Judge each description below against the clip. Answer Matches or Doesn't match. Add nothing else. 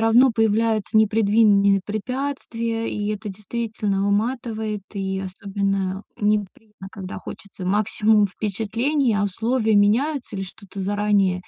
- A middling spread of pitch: Doesn't match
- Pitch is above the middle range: Matches